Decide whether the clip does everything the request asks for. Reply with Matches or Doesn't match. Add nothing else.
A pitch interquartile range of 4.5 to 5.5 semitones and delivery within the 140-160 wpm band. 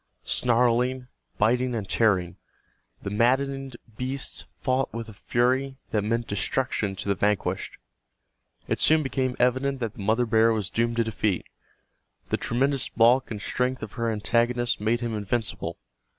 Doesn't match